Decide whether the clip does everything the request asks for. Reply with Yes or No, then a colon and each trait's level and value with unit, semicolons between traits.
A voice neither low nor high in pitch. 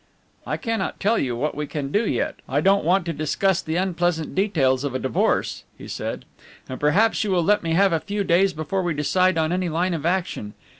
Yes: medium, 170 Hz